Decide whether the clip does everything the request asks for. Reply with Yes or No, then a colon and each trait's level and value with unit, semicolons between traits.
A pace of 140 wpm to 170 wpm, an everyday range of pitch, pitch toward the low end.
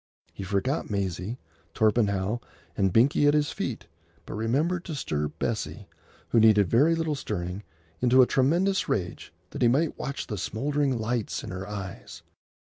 No: average, 155 wpm; wide, 6.3 semitones; low, 115 Hz